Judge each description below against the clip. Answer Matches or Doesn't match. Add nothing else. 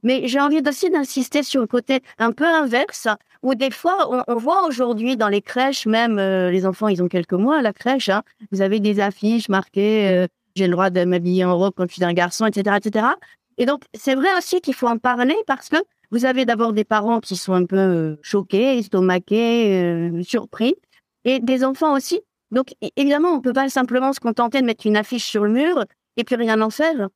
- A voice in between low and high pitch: Doesn't match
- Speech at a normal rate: Doesn't match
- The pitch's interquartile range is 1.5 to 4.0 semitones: Doesn't match